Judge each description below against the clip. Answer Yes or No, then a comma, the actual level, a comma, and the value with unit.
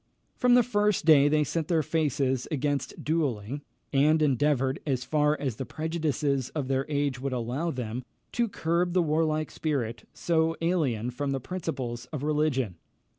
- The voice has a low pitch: No, medium, 145 Hz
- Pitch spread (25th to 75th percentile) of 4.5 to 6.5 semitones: No, average, 3.5 semitones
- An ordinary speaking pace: Yes, average, 155 wpm